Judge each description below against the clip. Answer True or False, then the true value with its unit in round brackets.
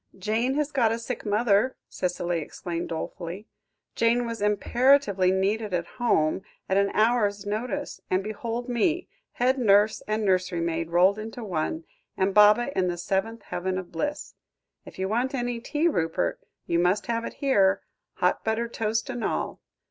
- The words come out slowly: False (165 wpm)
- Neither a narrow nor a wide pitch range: True (4.2 semitones)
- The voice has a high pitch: True (210 Hz)